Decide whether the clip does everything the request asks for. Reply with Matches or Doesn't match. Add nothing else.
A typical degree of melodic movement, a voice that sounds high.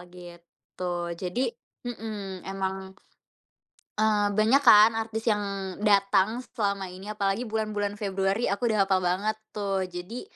Doesn't match